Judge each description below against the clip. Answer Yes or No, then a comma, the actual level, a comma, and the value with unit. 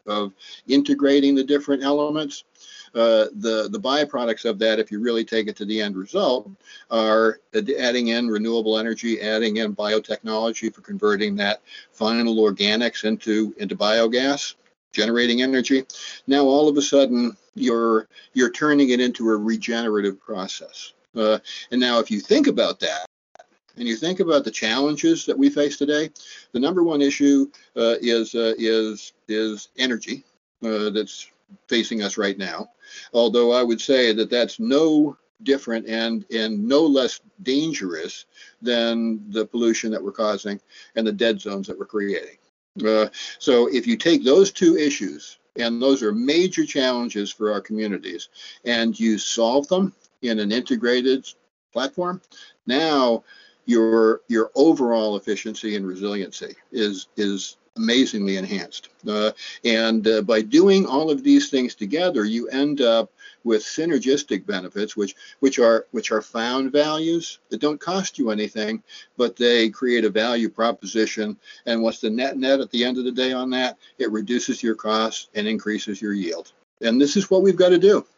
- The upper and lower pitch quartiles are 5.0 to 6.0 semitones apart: No, average, 4.2 semitones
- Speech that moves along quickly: No, average, 160 wpm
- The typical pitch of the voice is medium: No, low, 115 Hz